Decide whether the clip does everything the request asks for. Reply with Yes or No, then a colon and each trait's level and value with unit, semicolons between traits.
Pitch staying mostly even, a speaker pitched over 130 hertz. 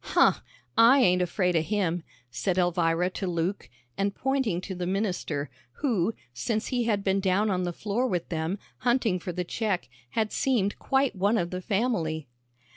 No: average, 4.0 semitones; high, 190 Hz